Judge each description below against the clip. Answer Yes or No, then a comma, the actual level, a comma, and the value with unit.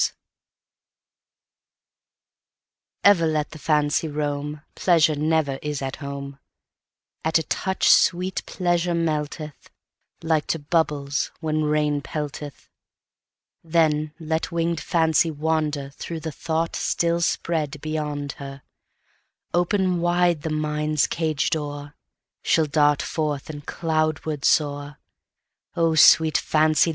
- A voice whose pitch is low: No, medium, 155 Hz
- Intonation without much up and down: Yes, narrow, 1.9 semitones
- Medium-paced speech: No, slow, 95 wpm